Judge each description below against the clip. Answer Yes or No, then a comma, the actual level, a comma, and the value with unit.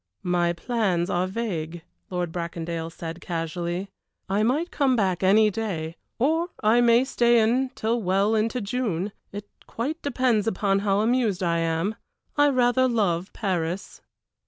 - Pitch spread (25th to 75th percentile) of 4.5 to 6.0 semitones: Yes, average, 5.3 semitones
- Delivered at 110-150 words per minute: Yes, average, 140 wpm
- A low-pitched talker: No, high, 205 Hz